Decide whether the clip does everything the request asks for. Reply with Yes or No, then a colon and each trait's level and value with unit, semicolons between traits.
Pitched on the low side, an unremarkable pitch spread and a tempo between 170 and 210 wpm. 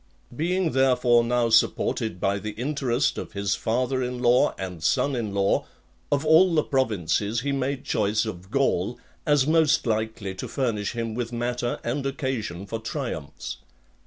No: low, 120 Hz; average, 4.2 semitones; average, 160 wpm